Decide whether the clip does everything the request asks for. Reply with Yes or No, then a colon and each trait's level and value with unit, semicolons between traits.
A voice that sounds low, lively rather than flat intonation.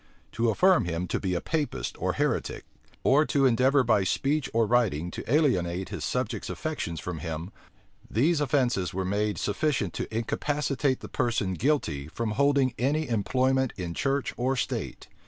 Yes: low, 120 Hz; wide, 6.8 semitones